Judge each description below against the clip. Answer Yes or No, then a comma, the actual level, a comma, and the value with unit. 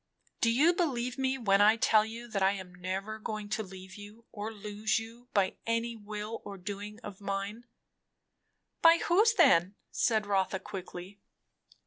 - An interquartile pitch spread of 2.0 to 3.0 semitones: Yes, average, 2.7 semitones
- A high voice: Yes, high, 210 Hz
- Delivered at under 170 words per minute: Yes, average, 160 wpm